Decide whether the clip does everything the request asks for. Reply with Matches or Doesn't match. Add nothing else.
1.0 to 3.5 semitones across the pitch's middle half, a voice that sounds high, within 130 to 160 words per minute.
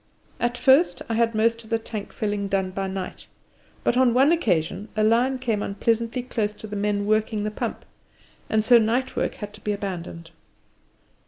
Doesn't match